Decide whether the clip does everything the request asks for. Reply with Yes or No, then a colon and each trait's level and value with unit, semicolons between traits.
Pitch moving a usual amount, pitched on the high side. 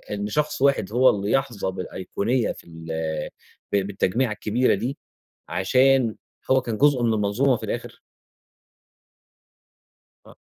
No: average, 4.6 semitones; low, 115 Hz